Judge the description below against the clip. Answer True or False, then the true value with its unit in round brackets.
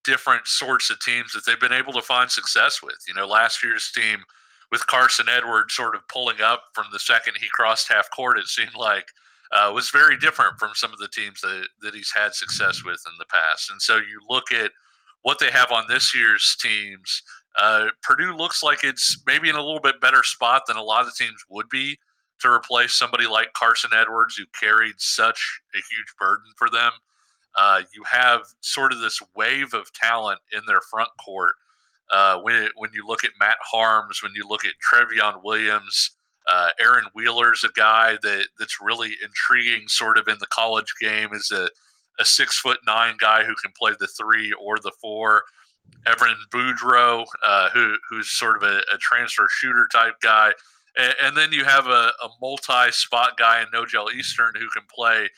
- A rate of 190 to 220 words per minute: True (200 wpm)